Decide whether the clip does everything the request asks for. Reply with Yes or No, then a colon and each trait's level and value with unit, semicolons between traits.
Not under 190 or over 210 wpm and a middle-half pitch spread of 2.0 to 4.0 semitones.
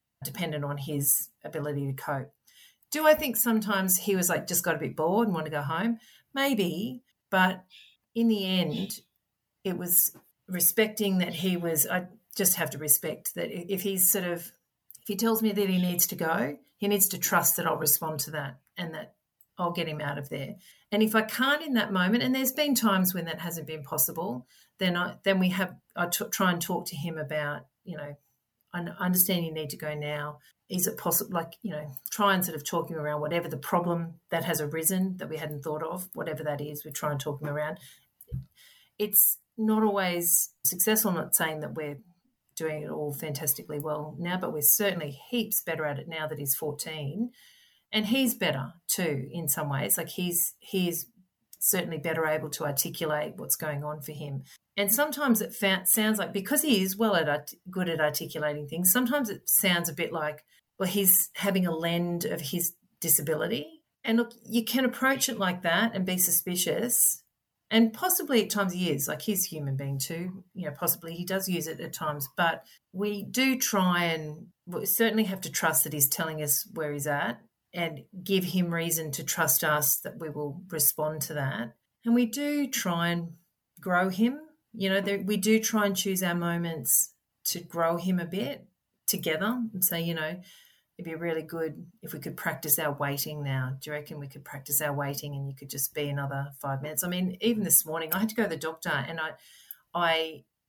No: fast, 205 wpm; average, 4.6 semitones